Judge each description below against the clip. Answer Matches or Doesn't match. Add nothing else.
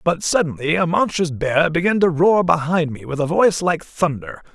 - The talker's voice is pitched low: Doesn't match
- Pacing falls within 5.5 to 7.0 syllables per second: Doesn't match